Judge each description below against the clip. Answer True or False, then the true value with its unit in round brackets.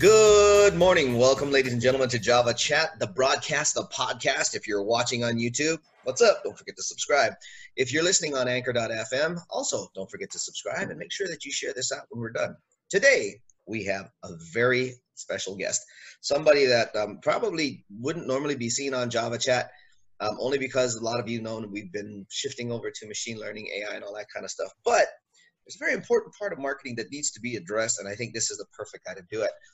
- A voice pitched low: True (125 Hz)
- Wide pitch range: True (6.2 semitones)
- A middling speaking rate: False (220 wpm)